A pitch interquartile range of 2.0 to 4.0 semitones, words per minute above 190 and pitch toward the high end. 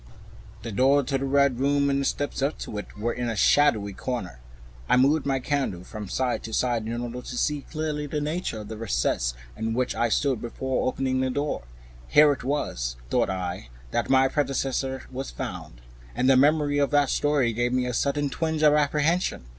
No: average, 3.7 semitones; average, 200 wpm; low, 130 Hz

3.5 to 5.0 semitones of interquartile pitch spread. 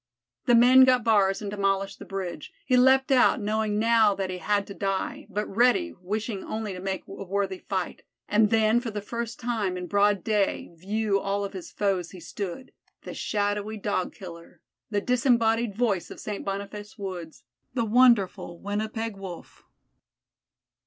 No: narrow, 2.5 semitones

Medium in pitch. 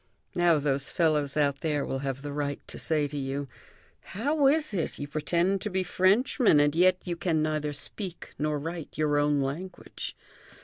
Yes: medium, 155 Hz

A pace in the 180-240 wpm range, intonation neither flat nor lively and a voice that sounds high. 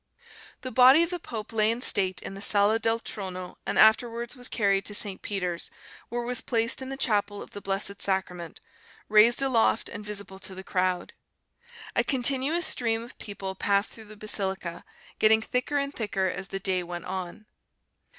Yes: average, 185 wpm; average, 3.7 semitones; high, 210 Hz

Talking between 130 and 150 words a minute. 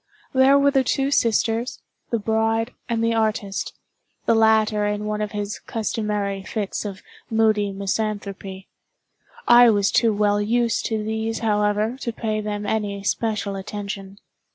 Yes: average, 140 wpm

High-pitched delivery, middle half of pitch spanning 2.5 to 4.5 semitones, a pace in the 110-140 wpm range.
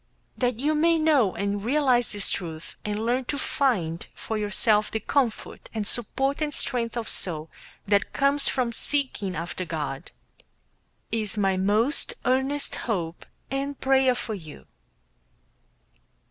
No: high, 230 Hz; average, 5.2 semitones; slow, 135 wpm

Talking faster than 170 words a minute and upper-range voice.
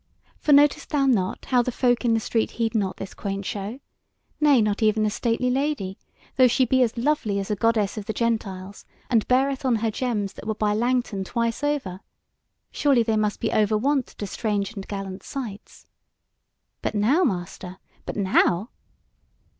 Yes: average, 180 wpm; high, 225 Hz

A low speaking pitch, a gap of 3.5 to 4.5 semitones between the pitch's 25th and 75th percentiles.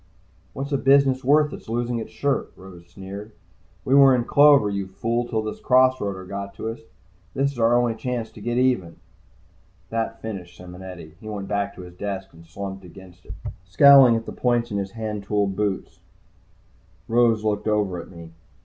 Yes: low, 110 Hz; average, 4.1 semitones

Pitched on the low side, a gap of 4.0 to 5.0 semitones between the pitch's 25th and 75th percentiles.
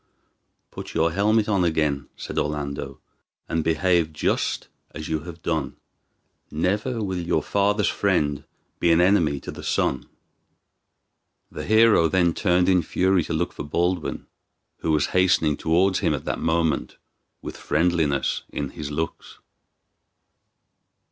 No: very low, 85 Hz; average, 3.3 semitones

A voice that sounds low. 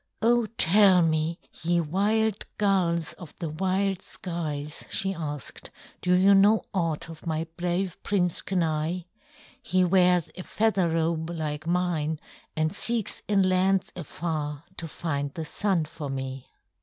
No: medium, 175 Hz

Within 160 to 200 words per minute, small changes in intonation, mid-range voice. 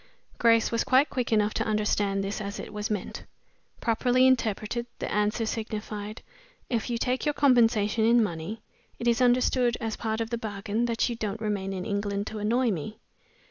No: average, 180 wpm; narrow, 2.3 semitones; high, 220 Hz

